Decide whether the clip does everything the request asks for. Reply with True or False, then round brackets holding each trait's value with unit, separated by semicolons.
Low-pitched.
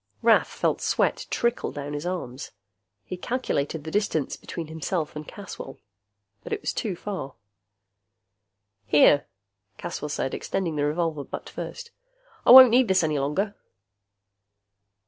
False (160 Hz)